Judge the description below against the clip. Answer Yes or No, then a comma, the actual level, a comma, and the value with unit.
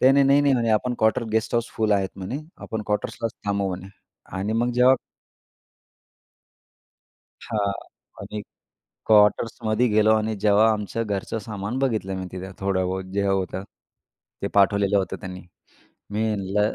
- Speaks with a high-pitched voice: No, low, 105 Hz